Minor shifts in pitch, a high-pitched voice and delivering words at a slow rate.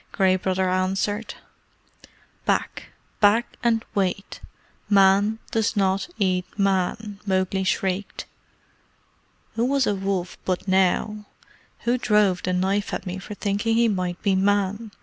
Yes: narrow, 2.0 semitones; high, 195 Hz; slow, 130 wpm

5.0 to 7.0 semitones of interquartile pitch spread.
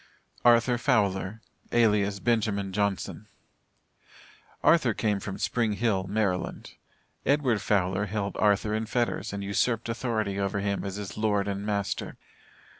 No: narrow, 2.4 semitones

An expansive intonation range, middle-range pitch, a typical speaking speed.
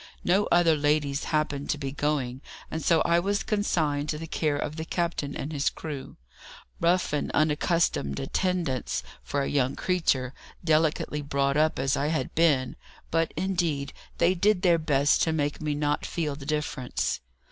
No: average, 2.9 semitones; medium, 150 Hz; average, 170 wpm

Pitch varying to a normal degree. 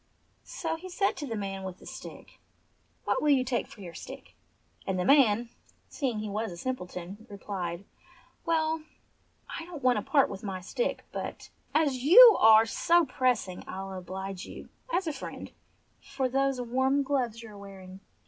No: wide, 6.4 semitones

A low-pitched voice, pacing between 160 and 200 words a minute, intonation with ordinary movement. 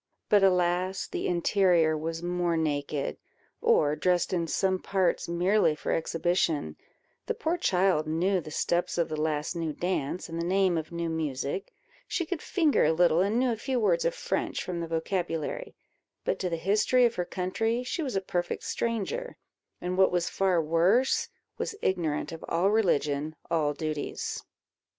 No: medium, 175 Hz; average, 170 wpm; average, 3.3 semitones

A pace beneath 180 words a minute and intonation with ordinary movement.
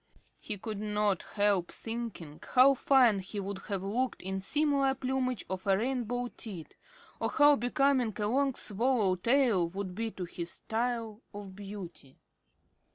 Yes: average, 150 wpm; average, 4.7 semitones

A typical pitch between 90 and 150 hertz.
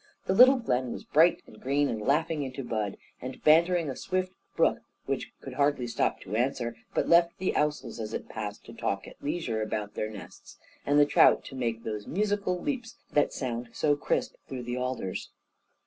Yes: low, 135 Hz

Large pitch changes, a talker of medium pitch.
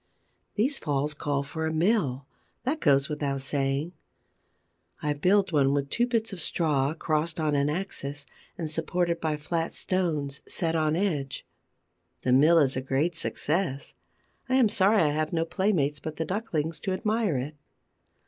No: average, 4.2 semitones; medium, 155 Hz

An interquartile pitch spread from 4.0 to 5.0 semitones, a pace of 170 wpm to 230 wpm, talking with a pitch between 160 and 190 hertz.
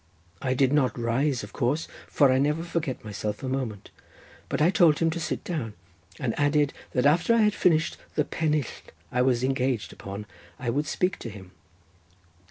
No: average, 4.3 semitones; average, 180 wpm; low, 135 Hz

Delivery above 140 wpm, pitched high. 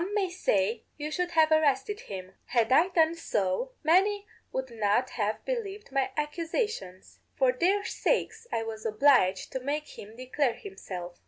Yes: average, 160 wpm; very high, 280 Hz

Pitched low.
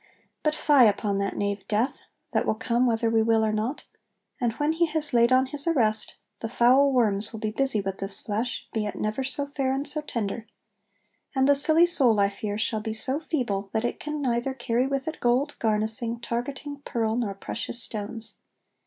No: high, 235 Hz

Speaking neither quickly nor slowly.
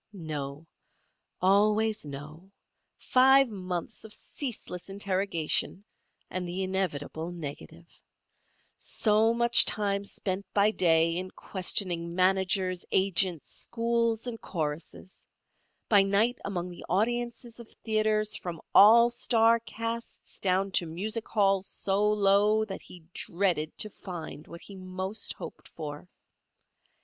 No: slow, 115 wpm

